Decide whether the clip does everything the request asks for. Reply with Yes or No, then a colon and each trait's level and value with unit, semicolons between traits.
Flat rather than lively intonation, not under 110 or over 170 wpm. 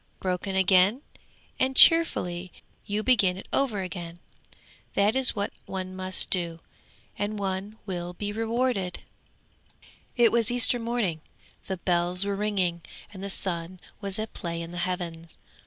No: average, 3.3 semitones; average, 140 wpm